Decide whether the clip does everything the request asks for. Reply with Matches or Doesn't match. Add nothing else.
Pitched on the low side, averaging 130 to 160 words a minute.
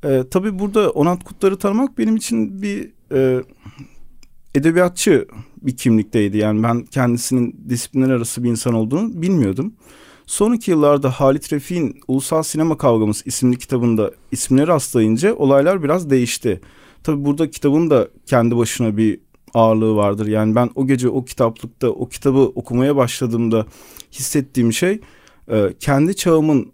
Matches